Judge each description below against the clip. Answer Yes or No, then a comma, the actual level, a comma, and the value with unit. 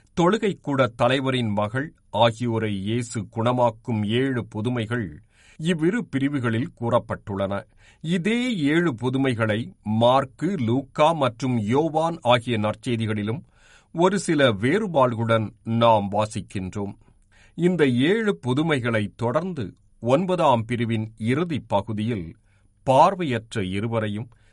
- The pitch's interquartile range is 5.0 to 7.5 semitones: No, average, 4.3 semitones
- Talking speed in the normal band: Yes, average, 85 wpm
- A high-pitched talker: No, low, 120 Hz